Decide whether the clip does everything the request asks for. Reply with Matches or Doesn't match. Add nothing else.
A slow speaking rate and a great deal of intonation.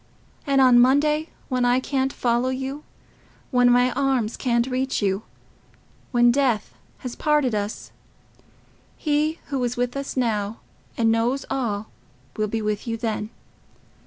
Doesn't match